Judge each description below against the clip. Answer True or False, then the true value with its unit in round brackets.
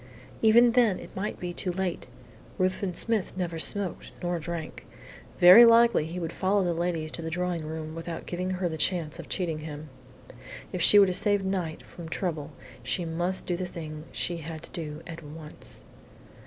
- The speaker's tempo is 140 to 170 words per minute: False (185 wpm)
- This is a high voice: False (175 Hz)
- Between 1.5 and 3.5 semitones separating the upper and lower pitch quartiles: True (2.6 semitones)